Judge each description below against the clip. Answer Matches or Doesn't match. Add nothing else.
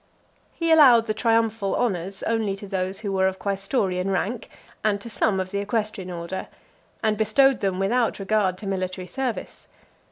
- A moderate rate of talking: Matches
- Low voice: Doesn't match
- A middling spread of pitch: Matches